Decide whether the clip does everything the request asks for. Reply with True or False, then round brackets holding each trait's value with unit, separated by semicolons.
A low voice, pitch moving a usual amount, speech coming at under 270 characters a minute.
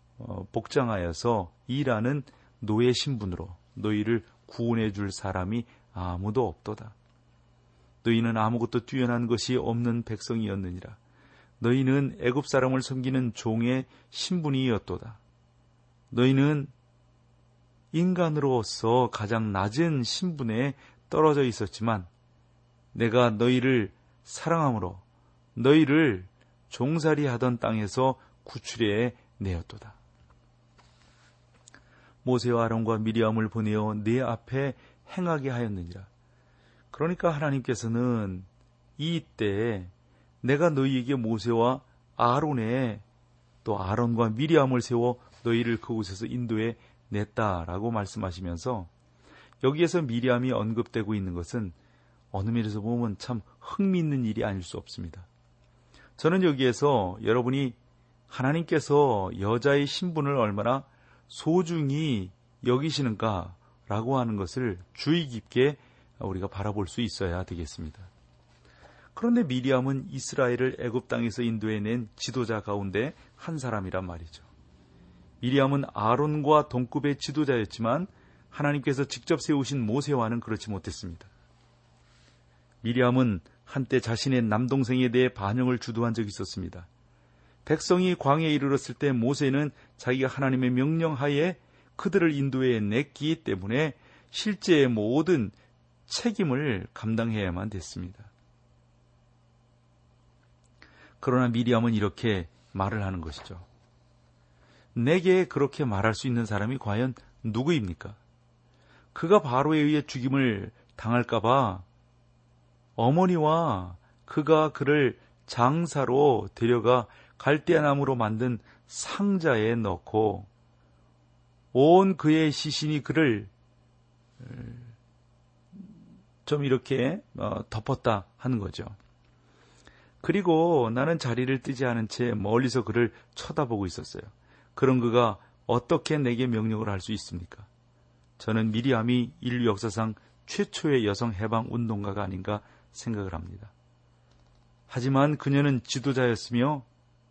True (120 Hz; 4.5 semitones; 255 characters per minute)